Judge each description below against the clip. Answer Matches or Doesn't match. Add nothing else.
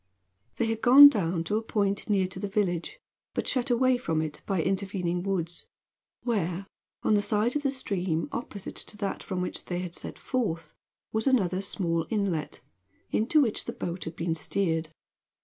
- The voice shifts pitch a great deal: Doesn't match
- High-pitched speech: Matches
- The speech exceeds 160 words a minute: Matches